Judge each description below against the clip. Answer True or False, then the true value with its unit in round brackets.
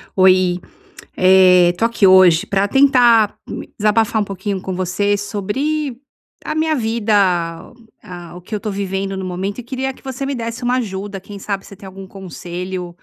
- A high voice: True (200 Hz)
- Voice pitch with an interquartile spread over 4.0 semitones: False (3.5 semitones)